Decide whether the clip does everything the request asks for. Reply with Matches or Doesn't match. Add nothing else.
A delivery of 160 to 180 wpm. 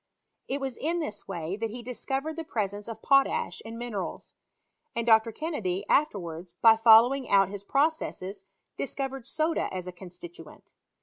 Matches